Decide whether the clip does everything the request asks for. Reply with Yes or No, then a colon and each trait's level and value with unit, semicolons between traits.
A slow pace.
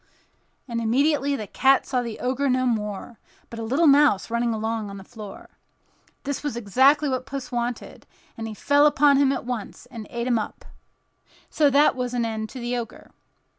No: average, 190 wpm